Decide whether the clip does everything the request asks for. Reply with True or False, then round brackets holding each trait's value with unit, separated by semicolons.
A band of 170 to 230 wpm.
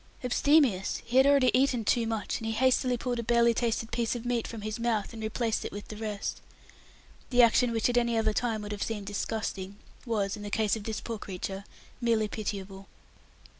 True (205 wpm)